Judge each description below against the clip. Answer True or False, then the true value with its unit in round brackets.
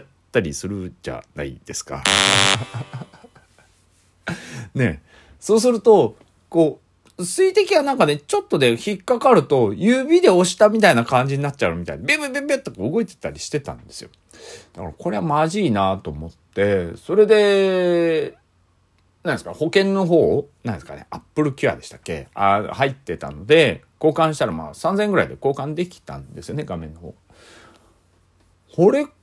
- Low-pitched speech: False (150 Hz)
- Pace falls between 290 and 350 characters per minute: True (320 characters per minute)